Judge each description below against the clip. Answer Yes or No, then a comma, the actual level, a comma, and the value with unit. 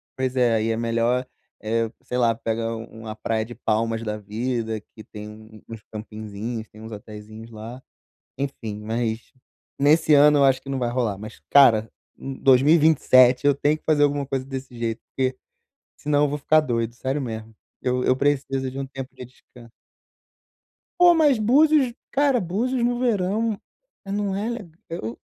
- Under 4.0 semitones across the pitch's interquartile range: No, average, 4.7 semitones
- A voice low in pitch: Yes, low, 125 Hz